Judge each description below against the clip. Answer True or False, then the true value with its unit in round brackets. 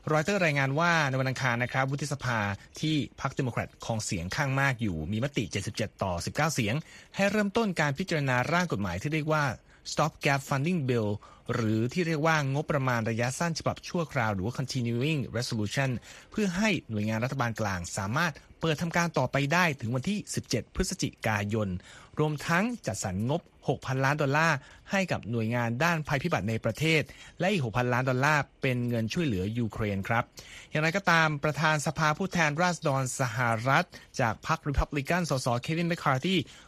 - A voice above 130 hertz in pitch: True (140 Hz)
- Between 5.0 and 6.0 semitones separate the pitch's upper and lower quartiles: True (5.4 semitones)